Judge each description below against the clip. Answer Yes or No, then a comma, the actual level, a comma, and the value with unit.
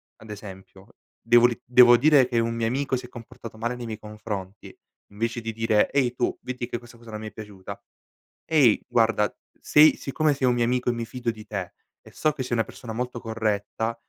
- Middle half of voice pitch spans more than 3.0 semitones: No, narrow, 2.4 semitones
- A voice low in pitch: Yes, low, 115 Hz